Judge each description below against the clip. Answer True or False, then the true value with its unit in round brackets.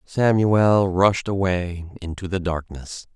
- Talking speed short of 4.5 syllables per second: True (3.5 syllables/s)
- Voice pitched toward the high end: False (95 Hz)